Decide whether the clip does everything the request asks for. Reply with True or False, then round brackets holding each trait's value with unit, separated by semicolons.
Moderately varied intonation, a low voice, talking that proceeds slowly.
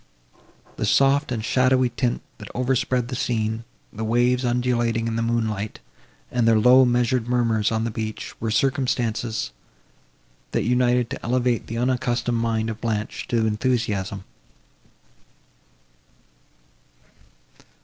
False (1.9 semitones; 120 Hz; 125 wpm)